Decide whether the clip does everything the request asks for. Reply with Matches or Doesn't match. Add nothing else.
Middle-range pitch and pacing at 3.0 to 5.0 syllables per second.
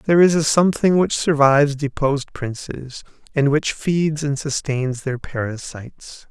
Matches